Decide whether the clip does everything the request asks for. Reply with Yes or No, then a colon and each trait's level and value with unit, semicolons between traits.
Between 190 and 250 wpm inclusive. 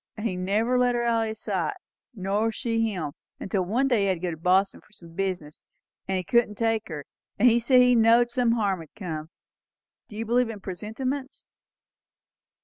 Yes: average, 200 wpm